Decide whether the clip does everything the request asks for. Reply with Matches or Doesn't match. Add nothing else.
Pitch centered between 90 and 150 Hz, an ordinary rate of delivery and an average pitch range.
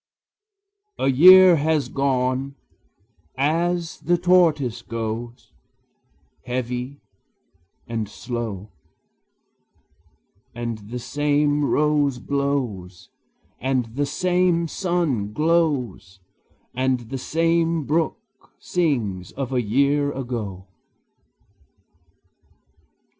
Doesn't match